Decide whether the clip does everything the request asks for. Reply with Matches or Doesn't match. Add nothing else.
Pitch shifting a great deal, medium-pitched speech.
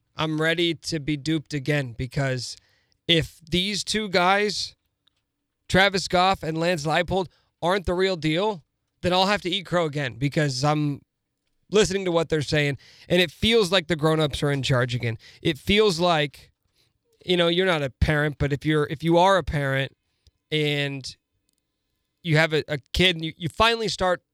Doesn't match